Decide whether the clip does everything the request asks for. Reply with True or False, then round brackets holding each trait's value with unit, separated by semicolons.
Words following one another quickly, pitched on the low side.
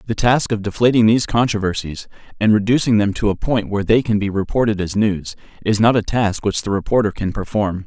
True (215 wpm; 105 Hz)